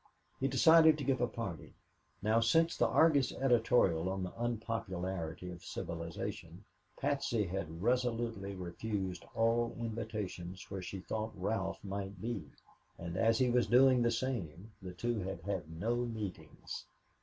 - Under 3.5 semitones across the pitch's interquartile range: No, average, 4.5 semitones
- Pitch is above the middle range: No, low, 110 Hz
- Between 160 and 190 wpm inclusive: No, average, 145 wpm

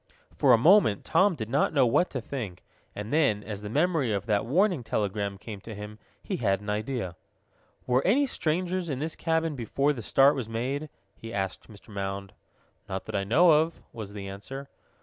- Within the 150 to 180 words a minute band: No, average, 195 wpm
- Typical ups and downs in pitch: No, wide, 6.6 semitones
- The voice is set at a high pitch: No, low, 120 Hz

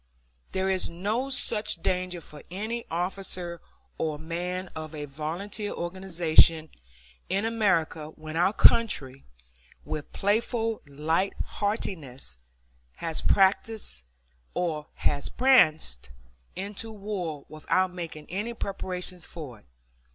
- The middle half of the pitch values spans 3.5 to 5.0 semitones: Yes, average, 4.5 semitones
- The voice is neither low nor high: Yes, medium, 175 Hz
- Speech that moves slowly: Yes, slow, 100 wpm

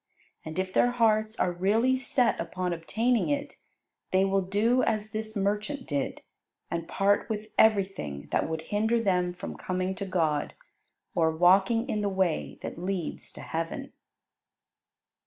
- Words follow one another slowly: No, average, 150 wpm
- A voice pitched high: Yes, high, 195 Hz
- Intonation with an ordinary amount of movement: Yes, average, 3.7 semitones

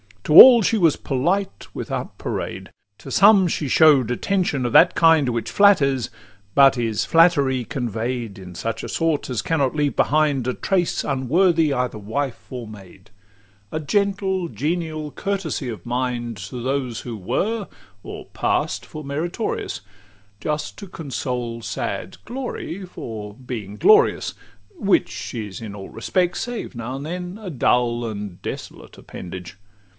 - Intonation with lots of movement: Yes, wide, 6.7 semitones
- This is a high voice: No, medium, 140 Hz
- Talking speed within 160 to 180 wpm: No, average, 150 wpm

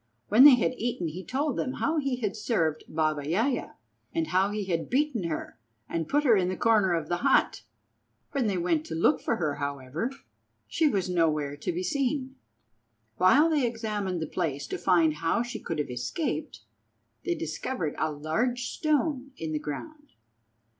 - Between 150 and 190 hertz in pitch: Yes, medium, 185 Hz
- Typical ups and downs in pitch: No, wide, 7.9 semitones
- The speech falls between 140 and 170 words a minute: No, average, 180 wpm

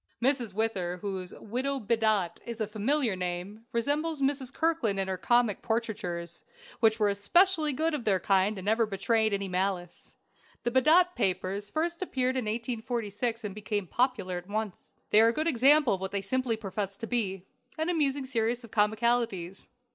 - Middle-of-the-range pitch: No, high, 220 Hz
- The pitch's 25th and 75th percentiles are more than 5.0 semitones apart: No, average, 4.5 semitones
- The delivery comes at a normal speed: Yes, average, 170 wpm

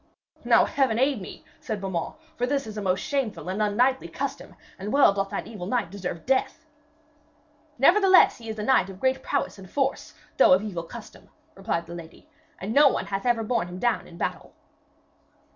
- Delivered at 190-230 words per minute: Yes, average, 195 wpm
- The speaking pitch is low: No, high, 215 Hz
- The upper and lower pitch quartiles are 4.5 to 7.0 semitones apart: Yes, wide, 5.4 semitones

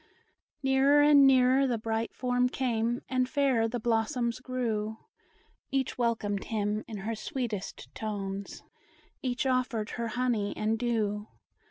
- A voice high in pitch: Yes, high, 235 Hz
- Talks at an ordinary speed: No, slow, 130 wpm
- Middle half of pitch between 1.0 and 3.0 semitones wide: Yes, average, 2.7 semitones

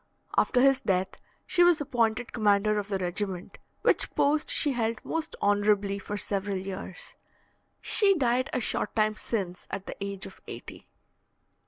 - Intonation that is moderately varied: Yes, average, 4.1 semitones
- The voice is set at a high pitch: Yes, high, 210 Hz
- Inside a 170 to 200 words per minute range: No, average, 155 wpm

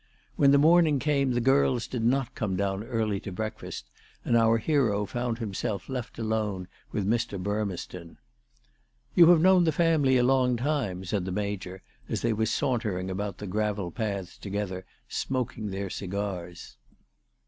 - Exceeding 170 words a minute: No, average, 160 wpm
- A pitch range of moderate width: Yes, average, 4.9 semitones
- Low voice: Yes, low, 110 Hz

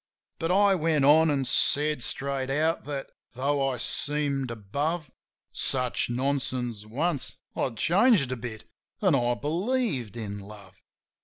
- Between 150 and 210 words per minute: No, slow, 135 wpm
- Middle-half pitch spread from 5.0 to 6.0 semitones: No, average, 4.4 semitones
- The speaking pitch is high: No, medium, 140 Hz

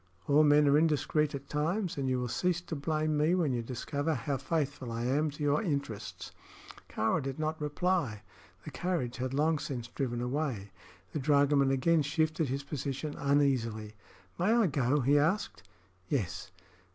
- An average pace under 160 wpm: No, average, 165 wpm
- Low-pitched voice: No, medium, 145 Hz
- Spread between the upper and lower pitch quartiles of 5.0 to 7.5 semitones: No, average, 3.1 semitones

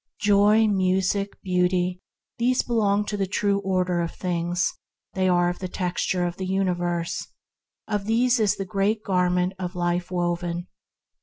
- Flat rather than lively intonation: Yes, narrow, 2.2 semitones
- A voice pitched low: No, medium, 185 Hz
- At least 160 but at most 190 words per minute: No, average, 150 wpm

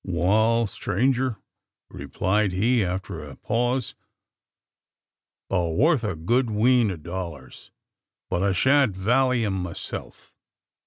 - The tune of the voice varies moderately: Yes, average, 5.0 semitones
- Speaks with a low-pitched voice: Yes, low, 105 Hz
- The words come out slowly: Yes, slow, 110 wpm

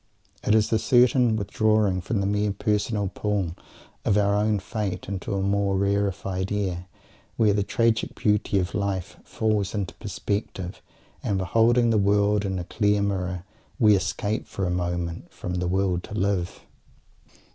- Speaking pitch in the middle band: No, low, 100 Hz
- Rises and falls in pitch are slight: Yes, narrow, 2.0 semitones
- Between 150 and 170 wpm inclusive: Yes, average, 155 wpm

